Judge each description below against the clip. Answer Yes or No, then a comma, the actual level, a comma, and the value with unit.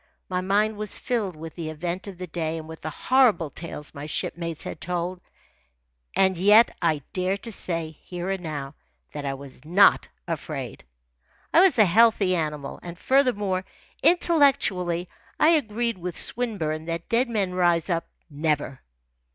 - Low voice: No, medium, 180 Hz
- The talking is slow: No, average, 160 wpm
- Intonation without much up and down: No, average, 4.6 semitones